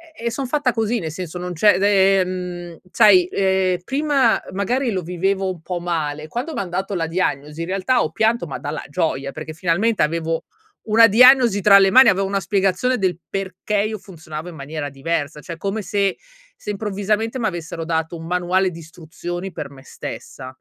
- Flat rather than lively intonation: No, average, 4.0 semitones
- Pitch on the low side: No, medium, 185 Hz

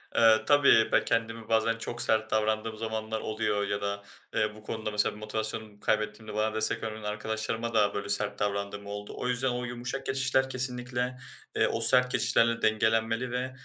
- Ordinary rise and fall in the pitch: No, narrow, 2.1 semitones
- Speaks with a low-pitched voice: Yes, low, 110 Hz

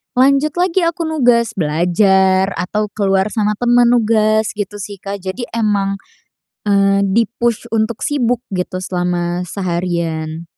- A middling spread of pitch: Yes, average, 4.1 semitones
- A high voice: Yes, high, 205 Hz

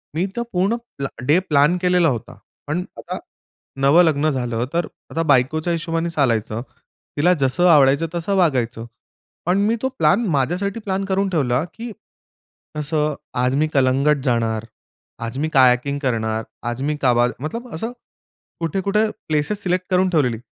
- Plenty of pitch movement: Yes, wide, 5.7 semitones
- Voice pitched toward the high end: No, medium, 150 Hz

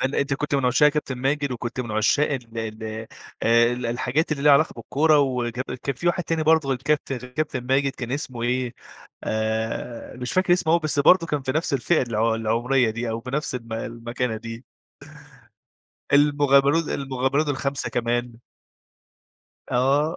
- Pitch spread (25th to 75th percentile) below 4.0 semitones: Yes, average, 3.5 semitones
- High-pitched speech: No, low, 130 Hz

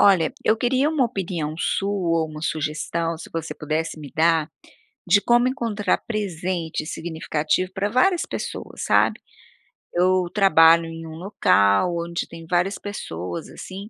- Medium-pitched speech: Yes, medium, 170 Hz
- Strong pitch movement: No, average, 3.9 semitones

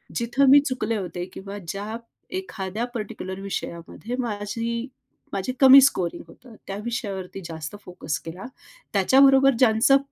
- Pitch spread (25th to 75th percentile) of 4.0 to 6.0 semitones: Yes, average, 4.7 semitones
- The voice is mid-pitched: No, high, 210 Hz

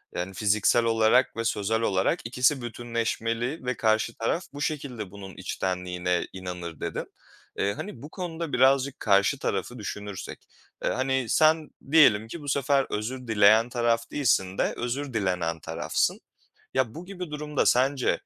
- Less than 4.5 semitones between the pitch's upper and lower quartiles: No, average, 5.1 semitones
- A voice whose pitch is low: Yes, low, 115 Hz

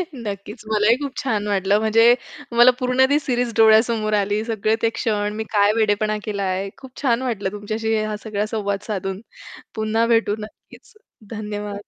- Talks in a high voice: Yes, high, 215 Hz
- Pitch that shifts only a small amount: Yes, narrow, 1.8 semitones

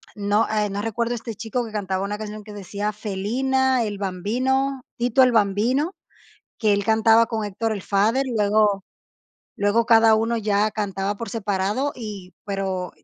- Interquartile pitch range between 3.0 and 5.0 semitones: No, narrow, 2.4 semitones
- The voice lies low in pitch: No, high, 215 Hz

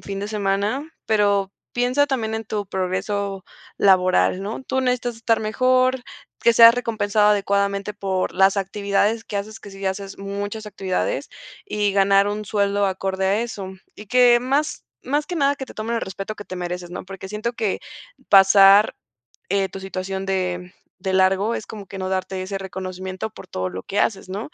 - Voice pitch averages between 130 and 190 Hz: No, high, 200 Hz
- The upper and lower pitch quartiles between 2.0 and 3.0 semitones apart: Yes, narrow, 2.5 semitones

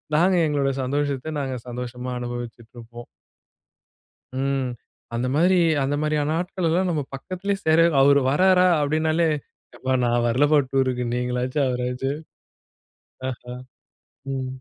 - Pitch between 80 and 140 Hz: Yes, low, 135 Hz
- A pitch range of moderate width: Yes, average, 4.0 semitones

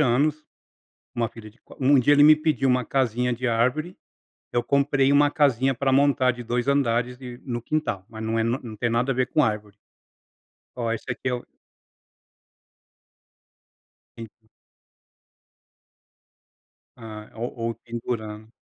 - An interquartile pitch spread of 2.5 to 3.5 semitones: Yes, average, 3.1 semitones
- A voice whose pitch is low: Yes, low, 125 Hz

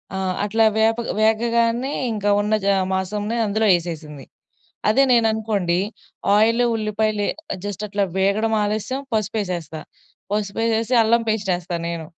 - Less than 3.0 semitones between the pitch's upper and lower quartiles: Yes, narrow, 2.4 semitones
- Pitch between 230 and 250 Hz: No, high, 215 Hz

